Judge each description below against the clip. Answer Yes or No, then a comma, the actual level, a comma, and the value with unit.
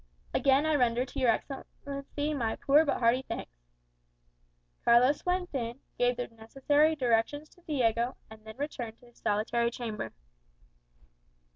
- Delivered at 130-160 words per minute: Yes, average, 140 wpm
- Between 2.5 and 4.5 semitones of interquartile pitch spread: Yes, average, 3.7 semitones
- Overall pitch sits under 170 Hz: No, high, 245 Hz